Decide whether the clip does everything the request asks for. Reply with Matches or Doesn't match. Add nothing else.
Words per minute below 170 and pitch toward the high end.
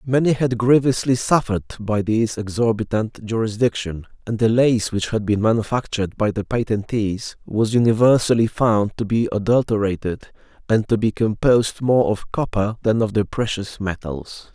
Doesn't match